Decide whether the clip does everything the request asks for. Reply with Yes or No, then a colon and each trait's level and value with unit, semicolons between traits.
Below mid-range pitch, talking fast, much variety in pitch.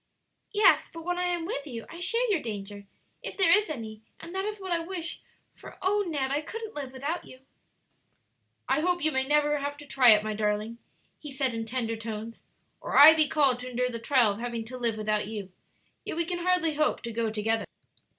No: very high, 270 Hz; fast, 220 wpm; wide, 6.7 semitones